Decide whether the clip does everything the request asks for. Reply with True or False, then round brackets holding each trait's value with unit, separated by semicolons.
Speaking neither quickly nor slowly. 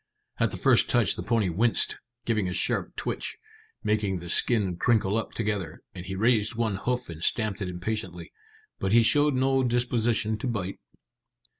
True (170 wpm)